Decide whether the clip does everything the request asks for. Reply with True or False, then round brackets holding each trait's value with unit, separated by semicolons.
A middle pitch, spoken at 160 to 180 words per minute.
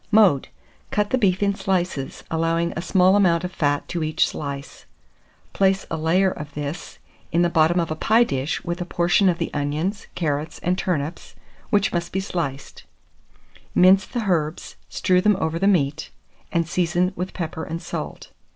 True (175 Hz; 175 wpm)